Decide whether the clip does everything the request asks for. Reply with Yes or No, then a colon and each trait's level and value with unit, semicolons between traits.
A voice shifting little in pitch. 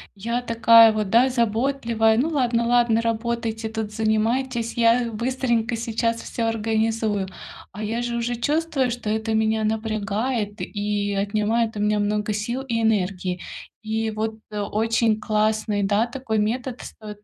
Yes: narrow, 1.8 semitones